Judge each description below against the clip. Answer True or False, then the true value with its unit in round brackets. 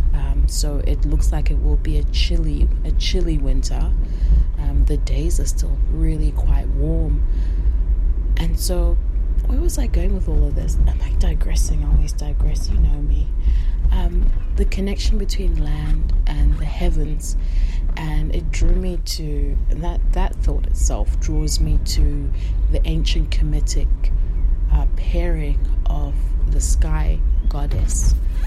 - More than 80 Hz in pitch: False (75 Hz)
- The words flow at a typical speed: True (145 wpm)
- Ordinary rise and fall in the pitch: False (2.3 semitones)